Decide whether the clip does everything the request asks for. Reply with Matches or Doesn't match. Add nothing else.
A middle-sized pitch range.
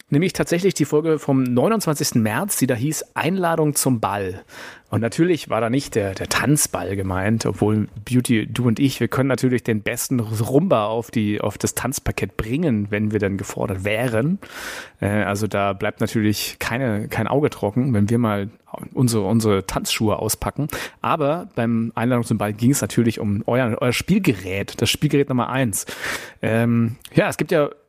Matches